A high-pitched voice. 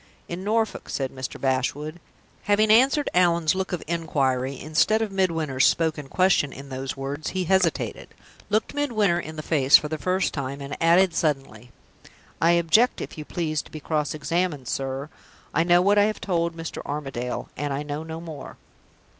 No: medium, 160 Hz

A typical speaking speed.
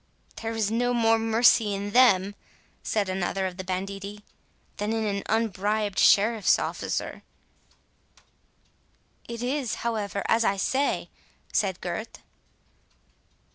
No: slow, 115 wpm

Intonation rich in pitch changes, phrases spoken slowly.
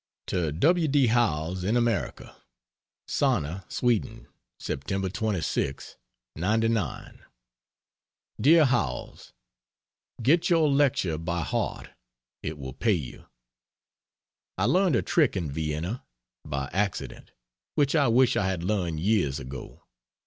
Yes: wide, 7.4 semitones; slow, 110 wpm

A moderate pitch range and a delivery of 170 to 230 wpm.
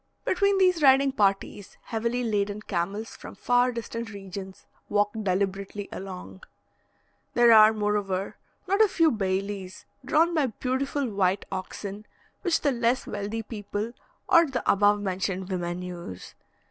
No: average, 4.2 semitones; slow, 135 wpm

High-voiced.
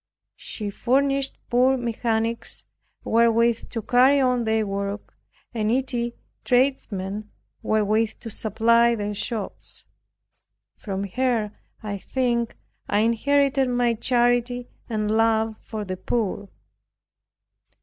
Yes: high, 230 Hz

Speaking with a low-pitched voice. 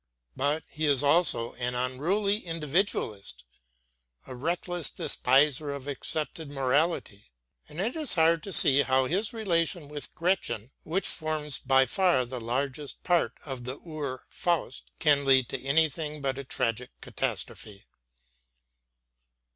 No: medium, 145 Hz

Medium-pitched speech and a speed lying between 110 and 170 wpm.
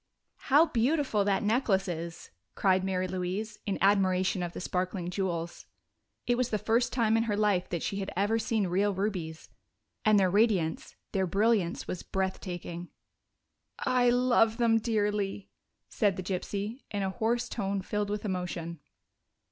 No: high, 200 Hz; average, 155 wpm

